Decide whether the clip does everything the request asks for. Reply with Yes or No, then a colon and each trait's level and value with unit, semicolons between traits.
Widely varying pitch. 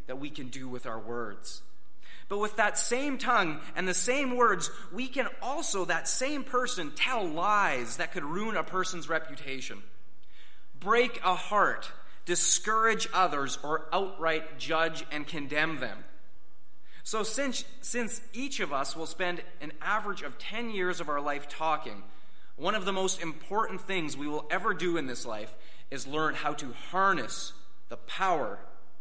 Yes: wide, 6.6 semitones